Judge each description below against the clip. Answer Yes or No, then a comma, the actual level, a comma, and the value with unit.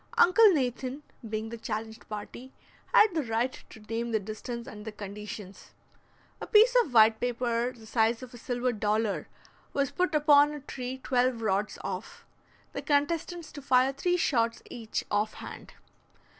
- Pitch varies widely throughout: No, average, 4.3 semitones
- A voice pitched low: No, high, 240 Hz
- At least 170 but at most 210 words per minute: No, average, 160 wpm